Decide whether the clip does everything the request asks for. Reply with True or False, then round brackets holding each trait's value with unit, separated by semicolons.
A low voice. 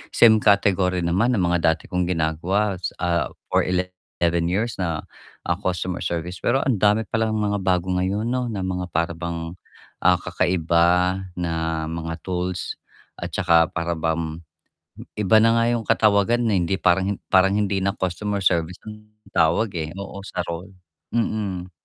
True (90 Hz)